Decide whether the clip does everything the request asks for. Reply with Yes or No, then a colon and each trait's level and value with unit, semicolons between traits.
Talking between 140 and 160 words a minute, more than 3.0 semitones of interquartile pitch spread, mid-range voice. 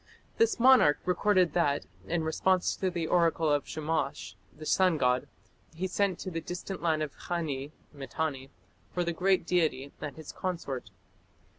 Yes: average, 155 wpm; average, 3.7 semitones; medium, 165 Hz